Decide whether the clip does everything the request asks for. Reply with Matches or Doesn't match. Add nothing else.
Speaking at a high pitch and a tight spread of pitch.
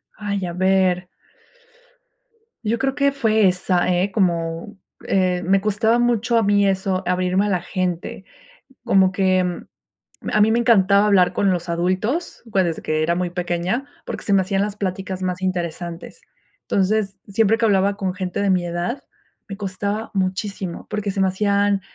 Matches